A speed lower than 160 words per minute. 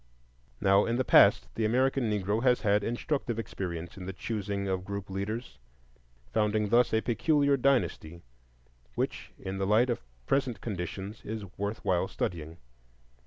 Yes: average, 150 wpm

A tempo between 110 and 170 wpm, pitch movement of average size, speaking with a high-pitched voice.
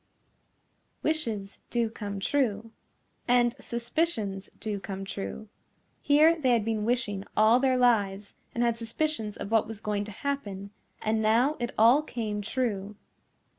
Yes: average, 140 wpm; average, 3.2 semitones; high, 225 Hz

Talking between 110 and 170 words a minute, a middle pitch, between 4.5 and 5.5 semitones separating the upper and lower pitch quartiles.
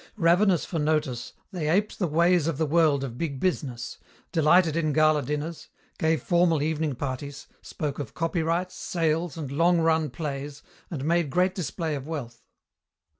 No: average, 160 wpm; medium, 160 Hz; average, 2.8 semitones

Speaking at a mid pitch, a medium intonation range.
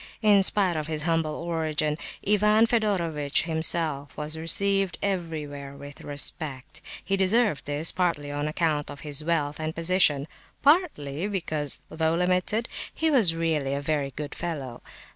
Yes: medium, 160 Hz; average, 4.0 semitones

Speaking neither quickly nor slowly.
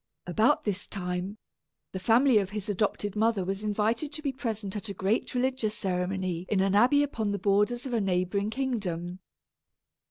Yes: average, 170 wpm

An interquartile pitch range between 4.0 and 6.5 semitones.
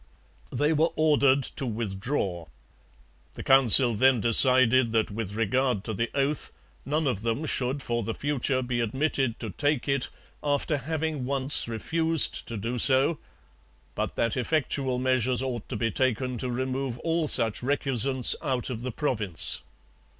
No: average, 3.2 semitones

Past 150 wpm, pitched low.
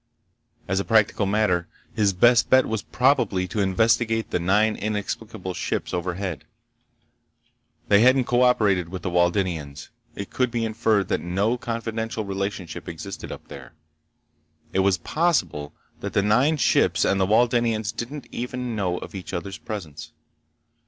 No: average, 145 wpm; low, 105 Hz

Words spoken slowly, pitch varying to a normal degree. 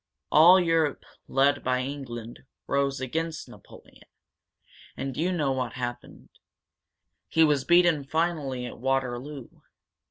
Yes: slow, 115 wpm; average, 3.8 semitones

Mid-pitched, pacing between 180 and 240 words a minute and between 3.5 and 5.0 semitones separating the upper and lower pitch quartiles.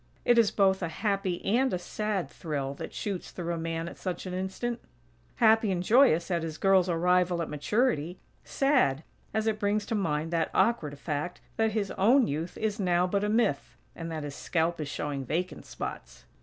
Yes: medium, 180 Hz; average, 195 wpm; average, 4.5 semitones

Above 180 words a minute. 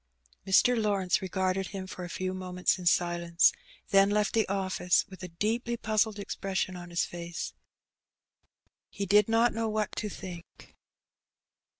No: average, 150 wpm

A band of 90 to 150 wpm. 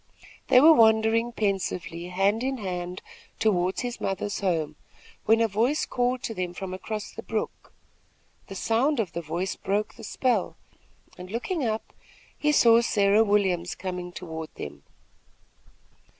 Yes: average, 145 wpm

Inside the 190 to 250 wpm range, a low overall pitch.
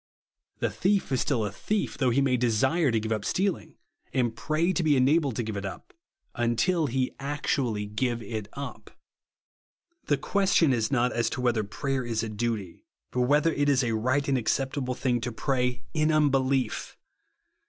No: average, 175 wpm; low, 130 Hz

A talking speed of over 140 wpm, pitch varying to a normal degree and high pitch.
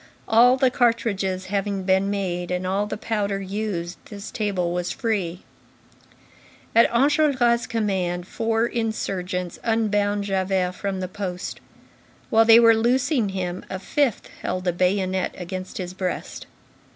No: slow, 135 wpm; average, 3.5 semitones; high, 200 Hz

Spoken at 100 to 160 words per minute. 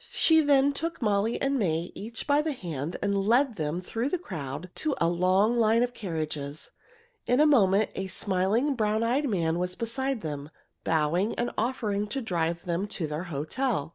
No: average, 180 wpm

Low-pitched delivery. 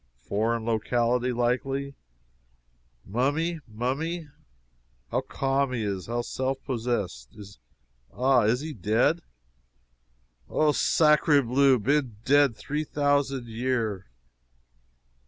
Yes: low, 125 Hz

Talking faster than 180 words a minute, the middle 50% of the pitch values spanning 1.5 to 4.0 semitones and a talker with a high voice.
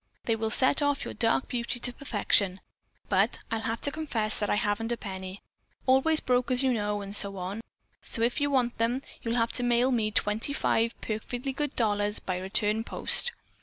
Yes: average, 190 wpm; average, 3.4 semitones; high, 230 Hz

